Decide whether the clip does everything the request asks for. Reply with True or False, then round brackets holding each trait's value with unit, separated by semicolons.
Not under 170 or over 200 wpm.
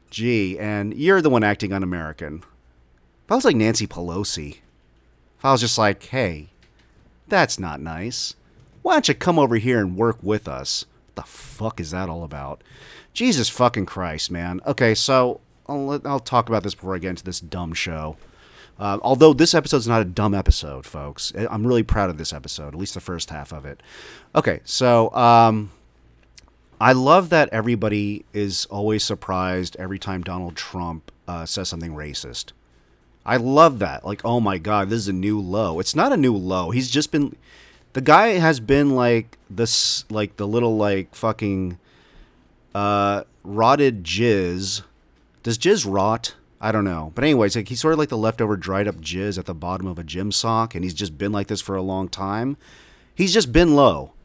True (190 wpm)